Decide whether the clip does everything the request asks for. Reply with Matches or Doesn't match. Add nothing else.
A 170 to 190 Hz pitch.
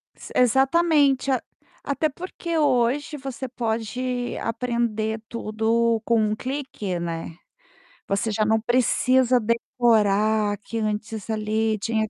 Doesn't match